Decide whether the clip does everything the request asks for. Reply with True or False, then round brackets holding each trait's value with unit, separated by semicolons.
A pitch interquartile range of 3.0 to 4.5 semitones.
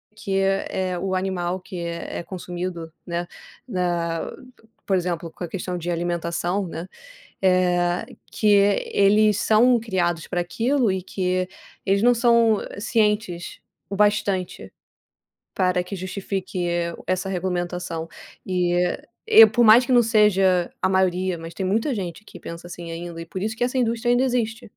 True (3.3 semitones)